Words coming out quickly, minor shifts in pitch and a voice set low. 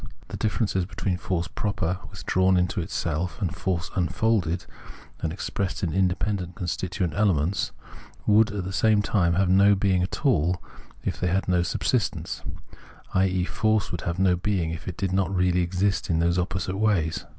No: average, 175 wpm; narrow, 2.2 semitones; very low, 95 Hz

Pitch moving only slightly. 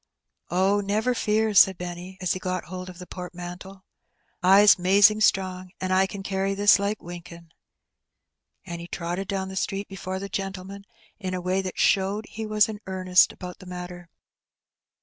Yes: narrow, 1.7 semitones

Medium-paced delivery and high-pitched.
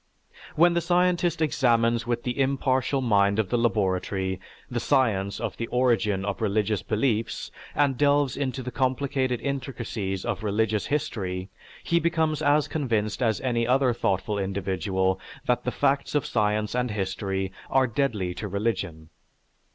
No: average, 145 wpm; low, 115 Hz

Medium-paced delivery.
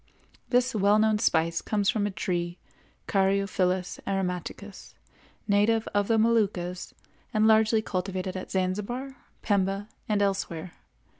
No: slow, 120 wpm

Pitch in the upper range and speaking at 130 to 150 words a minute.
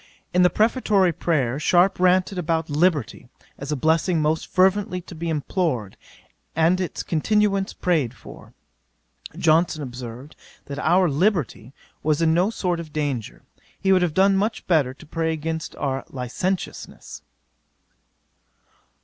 No: medium, 165 Hz; slow, 135 wpm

